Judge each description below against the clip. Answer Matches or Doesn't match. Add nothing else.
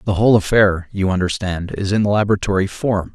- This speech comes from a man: Matches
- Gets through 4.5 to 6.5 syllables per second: Matches